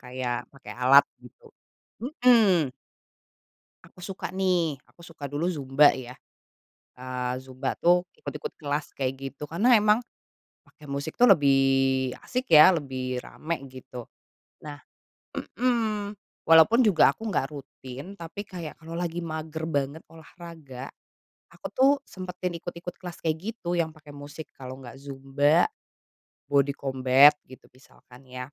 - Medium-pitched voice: Yes, medium, 150 Hz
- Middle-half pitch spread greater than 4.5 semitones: Yes, average, 4.9 semitones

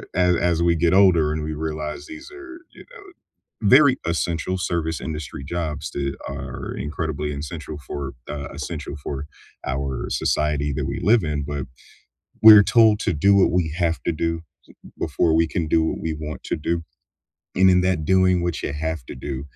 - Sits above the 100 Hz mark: No, very low, 80 Hz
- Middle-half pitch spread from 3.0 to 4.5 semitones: Yes, average, 3.6 semitones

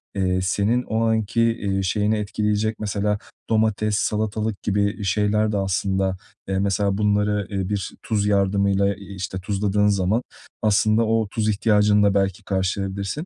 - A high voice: No, low, 105 Hz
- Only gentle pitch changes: Yes, narrow, 1.6 semitones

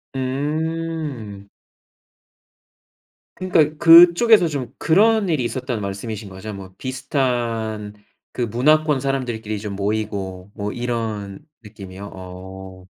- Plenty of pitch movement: Yes, wide, 6.6 semitones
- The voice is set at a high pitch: No, low, 115 Hz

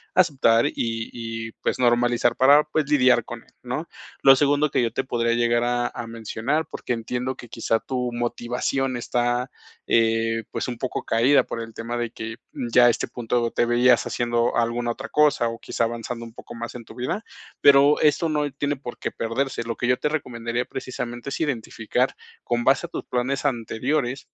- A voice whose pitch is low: Yes, low, 120 Hz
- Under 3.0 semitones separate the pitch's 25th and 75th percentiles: Yes, narrow, 2.4 semitones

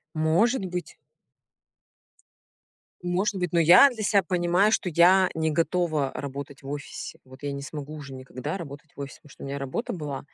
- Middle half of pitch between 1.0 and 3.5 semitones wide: No, average, 4.3 semitones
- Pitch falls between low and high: Yes, medium, 160 Hz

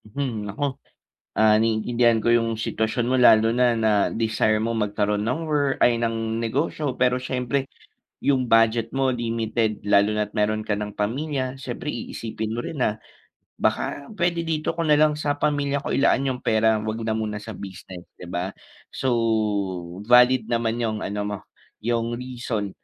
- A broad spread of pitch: No, average, 3.2 semitones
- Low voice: Yes, low, 115 Hz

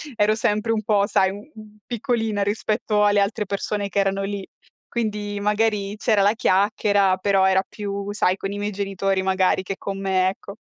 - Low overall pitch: No, high, 205 Hz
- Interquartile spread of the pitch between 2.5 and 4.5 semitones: No, narrow, 1.3 semitones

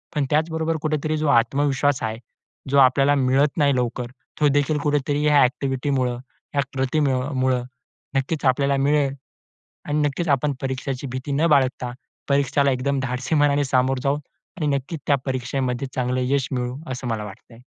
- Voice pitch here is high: No, low, 135 Hz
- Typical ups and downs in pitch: No, narrow, 2.2 semitones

